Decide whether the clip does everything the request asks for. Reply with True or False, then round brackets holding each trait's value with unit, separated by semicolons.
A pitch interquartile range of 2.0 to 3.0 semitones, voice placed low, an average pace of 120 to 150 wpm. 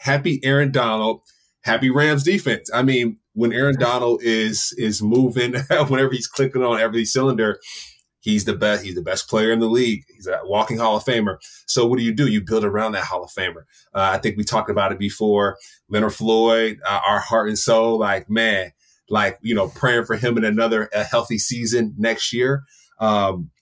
False (2.5 semitones; 115 Hz; 200 wpm)